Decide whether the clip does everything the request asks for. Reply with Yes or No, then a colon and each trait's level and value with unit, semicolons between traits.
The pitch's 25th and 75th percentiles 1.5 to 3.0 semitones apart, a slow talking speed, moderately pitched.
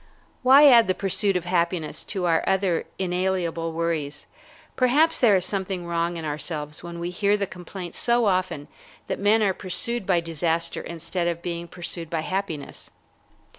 No: average, 2.7 semitones; average, 165 wpm; medium, 180 Hz